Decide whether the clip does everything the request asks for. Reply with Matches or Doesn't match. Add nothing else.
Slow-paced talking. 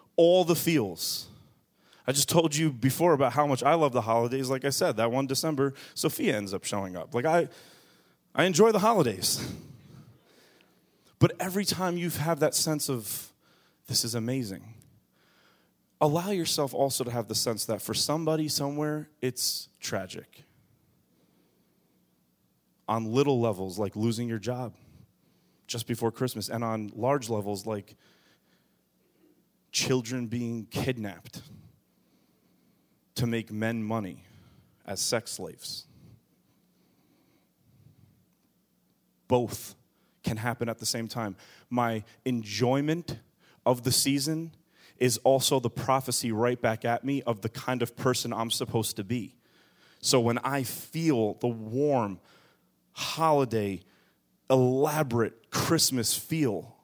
Matches